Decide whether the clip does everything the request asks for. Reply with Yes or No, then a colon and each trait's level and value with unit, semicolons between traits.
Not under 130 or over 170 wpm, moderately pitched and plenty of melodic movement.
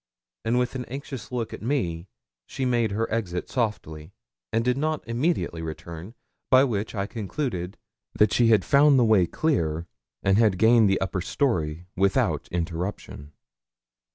No: average, 155 wpm; low, 110 Hz; wide, 5.8 semitones